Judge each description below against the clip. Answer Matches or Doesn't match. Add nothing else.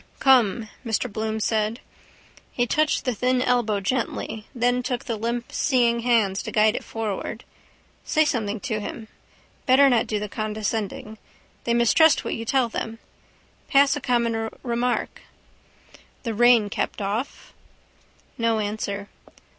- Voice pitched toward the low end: Doesn't match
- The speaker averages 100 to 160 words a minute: Matches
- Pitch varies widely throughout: Doesn't match